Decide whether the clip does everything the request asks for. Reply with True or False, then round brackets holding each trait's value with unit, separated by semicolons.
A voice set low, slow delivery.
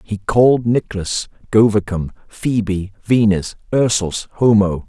True (105 Hz; 100 wpm)